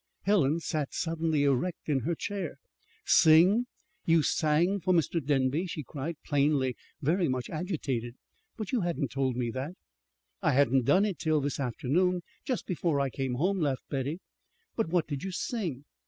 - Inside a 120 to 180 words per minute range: Yes, average, 165 wpm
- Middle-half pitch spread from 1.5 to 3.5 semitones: No, average, 4.7 semitones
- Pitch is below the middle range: No, medium, 155 Hz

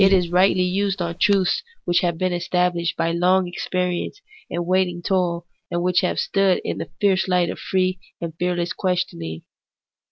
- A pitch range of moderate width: No, narrow, 1.3 semitones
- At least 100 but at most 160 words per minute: No, average, 170 wpm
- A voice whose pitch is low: No, medium, 180 Hz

